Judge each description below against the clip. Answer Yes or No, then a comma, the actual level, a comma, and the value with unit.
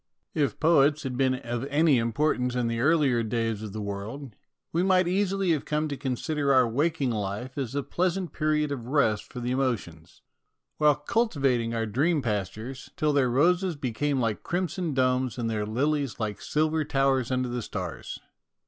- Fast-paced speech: No, average, 175 wpm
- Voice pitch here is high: No, low, 135 Hz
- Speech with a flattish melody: No, average, 4.6 semitones